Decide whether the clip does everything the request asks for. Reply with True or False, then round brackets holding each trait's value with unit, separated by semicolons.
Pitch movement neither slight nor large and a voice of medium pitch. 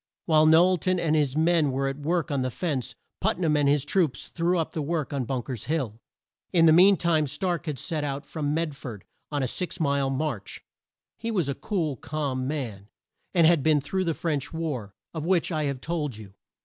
True (3.5 semitones; 150 Hz)